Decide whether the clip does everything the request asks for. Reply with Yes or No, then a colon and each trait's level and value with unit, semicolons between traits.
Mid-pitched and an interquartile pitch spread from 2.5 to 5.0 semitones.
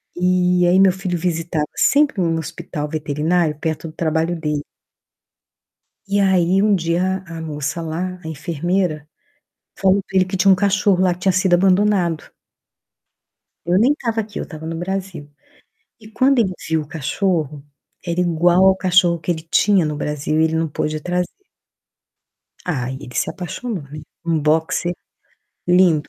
Yes: medium, 175 Hz; average, 3.0 semitones